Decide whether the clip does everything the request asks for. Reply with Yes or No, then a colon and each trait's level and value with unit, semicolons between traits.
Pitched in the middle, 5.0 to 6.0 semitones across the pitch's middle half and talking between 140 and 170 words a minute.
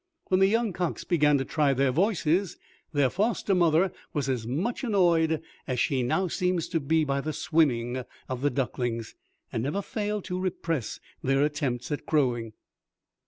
Yes: medium, 155 Hz; wide, 5.5 semitones; average, 165 wpm